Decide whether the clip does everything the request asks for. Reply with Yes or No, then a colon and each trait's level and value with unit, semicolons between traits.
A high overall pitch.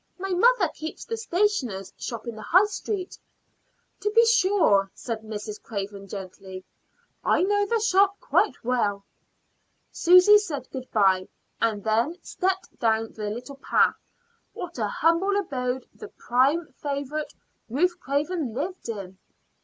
Yes: very high, 280 Hz